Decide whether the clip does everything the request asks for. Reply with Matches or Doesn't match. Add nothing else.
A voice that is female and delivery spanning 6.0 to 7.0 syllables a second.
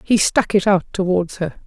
Doesn't match